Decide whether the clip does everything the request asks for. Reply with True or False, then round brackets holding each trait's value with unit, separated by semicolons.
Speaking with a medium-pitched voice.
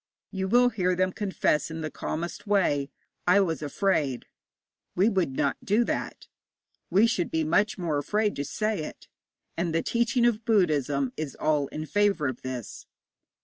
True (175 Hz)